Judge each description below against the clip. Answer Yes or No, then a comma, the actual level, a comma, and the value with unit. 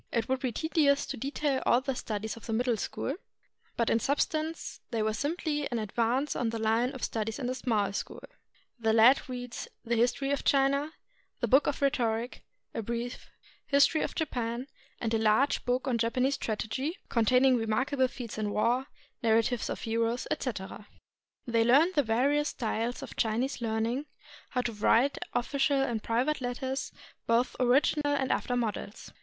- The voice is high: Yes, high, 245 Hz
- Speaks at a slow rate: No, average, 170 wpm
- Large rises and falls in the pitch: No, average, 3.2 semitones